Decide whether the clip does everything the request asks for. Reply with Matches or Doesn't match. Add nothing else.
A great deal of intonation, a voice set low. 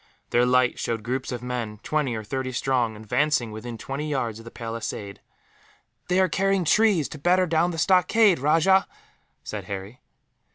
Matches